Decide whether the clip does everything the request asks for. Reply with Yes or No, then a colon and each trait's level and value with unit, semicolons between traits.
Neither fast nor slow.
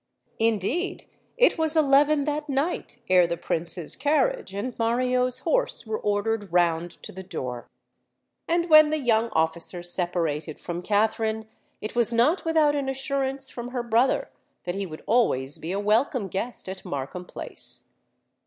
Yes: average, 155 wpm